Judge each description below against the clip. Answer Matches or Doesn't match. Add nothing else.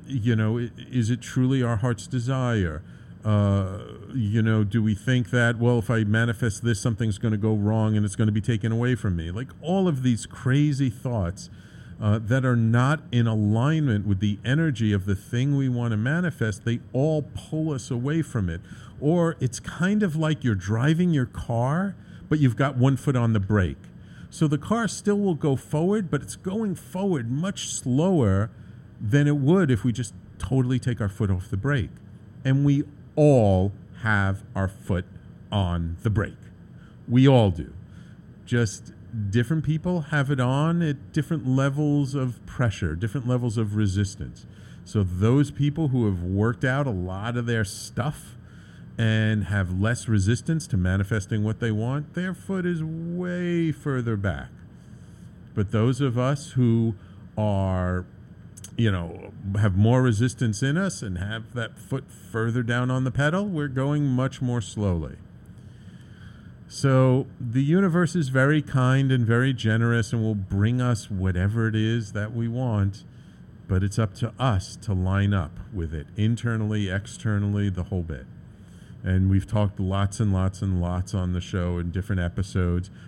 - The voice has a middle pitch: Doesn't match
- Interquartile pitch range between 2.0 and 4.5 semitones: Doesn't match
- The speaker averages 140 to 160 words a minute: Doesn't match